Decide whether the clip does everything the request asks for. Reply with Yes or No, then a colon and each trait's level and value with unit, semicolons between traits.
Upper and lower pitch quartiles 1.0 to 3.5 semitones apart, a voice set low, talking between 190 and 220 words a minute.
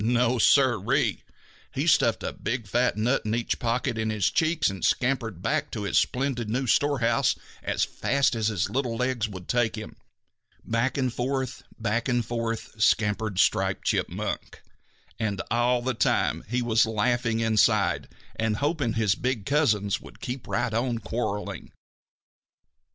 No: narrow, 2.5 semitones; low, 115 Hz; average, 155 wpm